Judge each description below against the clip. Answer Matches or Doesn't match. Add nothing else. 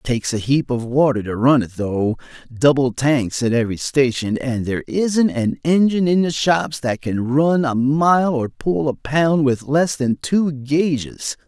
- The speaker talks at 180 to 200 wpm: Matches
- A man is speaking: Matches